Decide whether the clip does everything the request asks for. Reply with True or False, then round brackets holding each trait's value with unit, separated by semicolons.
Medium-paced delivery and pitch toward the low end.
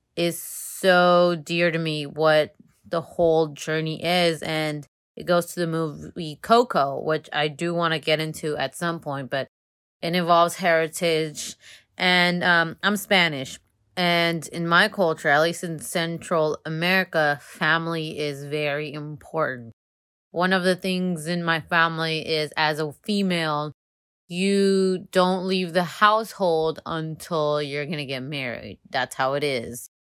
False (145 wpm; 160 Hz)